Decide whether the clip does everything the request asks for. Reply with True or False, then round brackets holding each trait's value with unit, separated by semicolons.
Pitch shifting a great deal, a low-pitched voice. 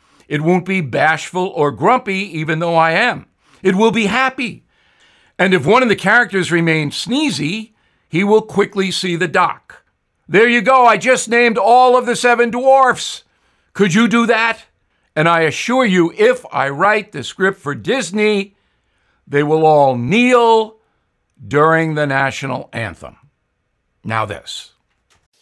False (7.6 semitones; 190 Hz)